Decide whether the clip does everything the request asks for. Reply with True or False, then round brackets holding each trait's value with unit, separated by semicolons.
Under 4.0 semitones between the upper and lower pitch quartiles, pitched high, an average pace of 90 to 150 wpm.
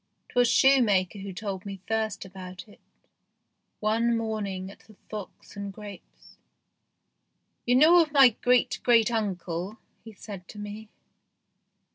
True (2.9 semitones; 210 Hz; 135 wpm)